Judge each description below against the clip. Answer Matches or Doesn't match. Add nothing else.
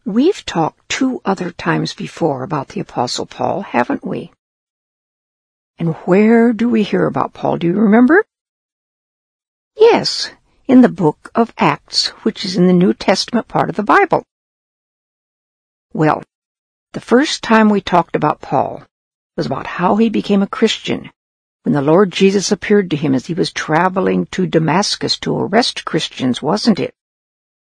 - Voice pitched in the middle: Doesn't match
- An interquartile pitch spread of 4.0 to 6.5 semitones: Matches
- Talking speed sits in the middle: Matches